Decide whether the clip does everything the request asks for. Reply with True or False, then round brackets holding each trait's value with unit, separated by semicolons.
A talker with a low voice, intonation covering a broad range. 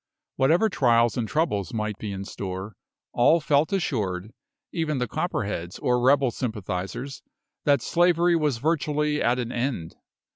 True (125 Hz; 6.0 semitones)